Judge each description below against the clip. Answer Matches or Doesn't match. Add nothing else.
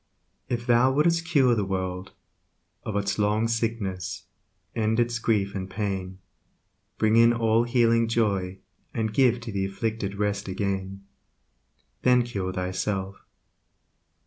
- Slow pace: Matches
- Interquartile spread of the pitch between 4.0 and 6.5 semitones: Doesn't match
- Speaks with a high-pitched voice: Doesn't match